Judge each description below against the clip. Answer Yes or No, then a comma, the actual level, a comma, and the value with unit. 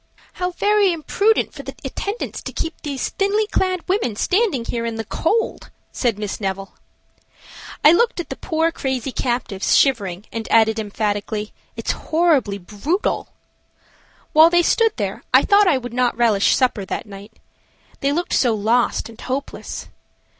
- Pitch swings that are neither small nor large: No, wide, 8.1 semitones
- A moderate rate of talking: Yes, average, 155 wpm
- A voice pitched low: No, very high, 260 Hz